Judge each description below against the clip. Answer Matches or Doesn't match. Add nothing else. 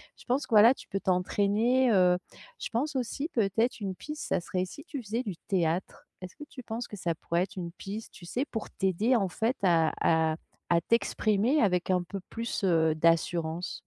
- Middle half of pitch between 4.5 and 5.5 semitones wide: Matches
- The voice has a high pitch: Matches